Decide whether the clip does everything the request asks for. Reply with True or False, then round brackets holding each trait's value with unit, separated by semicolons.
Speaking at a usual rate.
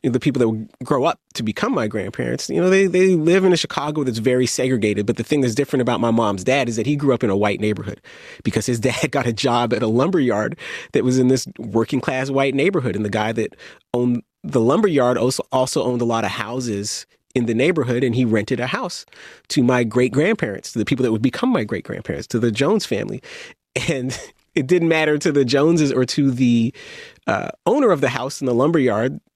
False (240 wpm)